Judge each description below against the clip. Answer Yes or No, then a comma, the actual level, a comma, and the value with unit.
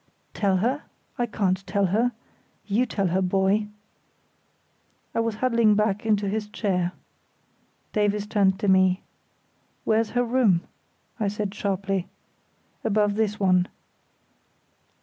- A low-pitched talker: No, high, 205 Hz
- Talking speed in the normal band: No, slow, 120 wpm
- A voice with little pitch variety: Yes, narrow, 2.2 semitones